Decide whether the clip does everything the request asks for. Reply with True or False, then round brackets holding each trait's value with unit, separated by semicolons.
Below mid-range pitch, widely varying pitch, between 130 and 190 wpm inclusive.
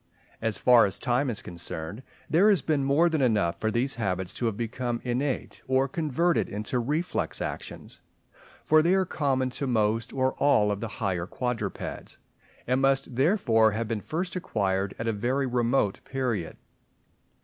False (125 Hz; 4.3 semitones; 165 wpm)